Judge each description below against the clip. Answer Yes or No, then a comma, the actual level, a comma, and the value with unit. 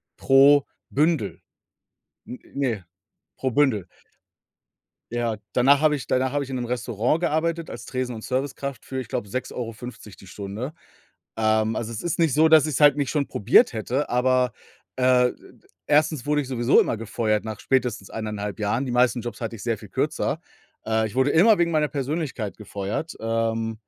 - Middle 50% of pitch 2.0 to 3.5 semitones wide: No, average, 4.3 semitones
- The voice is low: Yes, low, 125 Hz